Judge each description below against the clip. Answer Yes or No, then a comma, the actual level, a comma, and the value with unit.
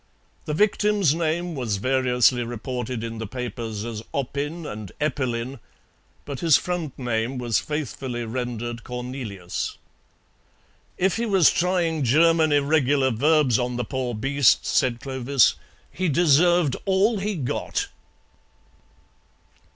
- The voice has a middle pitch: No, low, 130 Hz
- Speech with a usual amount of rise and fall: Yes, average, 4.8 semitones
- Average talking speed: No, slow, 120 wpm